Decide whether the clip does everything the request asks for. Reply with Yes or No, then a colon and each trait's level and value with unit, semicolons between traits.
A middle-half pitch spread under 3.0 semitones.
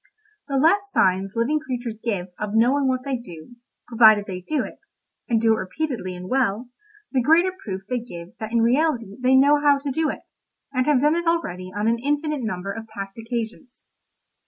No: average, 5.2 semitones